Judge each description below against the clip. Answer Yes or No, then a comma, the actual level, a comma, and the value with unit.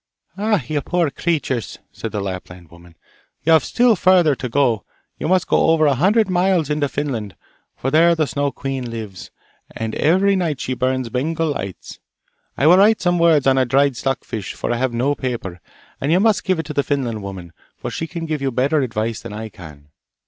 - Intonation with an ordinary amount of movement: No, wide, 6.1 semitones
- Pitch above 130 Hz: Yes, medium, 140 Hz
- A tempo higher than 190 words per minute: Yes, fast, 205 wpm